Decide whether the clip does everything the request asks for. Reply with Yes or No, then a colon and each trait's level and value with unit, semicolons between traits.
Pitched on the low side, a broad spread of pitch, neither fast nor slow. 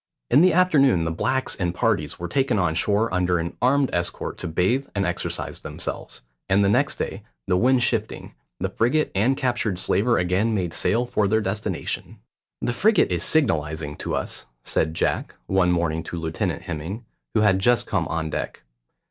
Yes: low, 100 Hz; wide, 6.0 semitones; average, 180 wpm